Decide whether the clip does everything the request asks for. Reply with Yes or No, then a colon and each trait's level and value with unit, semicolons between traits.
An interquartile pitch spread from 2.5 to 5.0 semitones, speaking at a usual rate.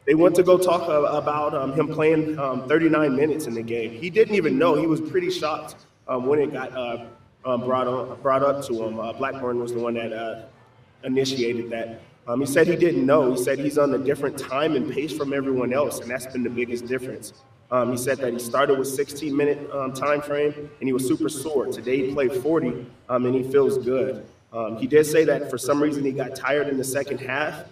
No: average, 3.2 semitones; fast, 235 wpm